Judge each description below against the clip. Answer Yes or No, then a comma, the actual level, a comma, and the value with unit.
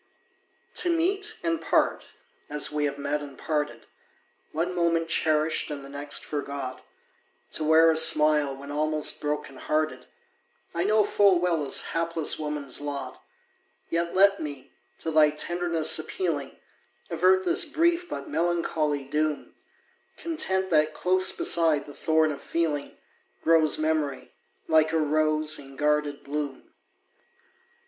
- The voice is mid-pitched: Yes, medium, 155 Hz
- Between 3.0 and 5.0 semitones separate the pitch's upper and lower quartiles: No, narrow, 2.5 semitones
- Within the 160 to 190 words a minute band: No, slow, 135 wpm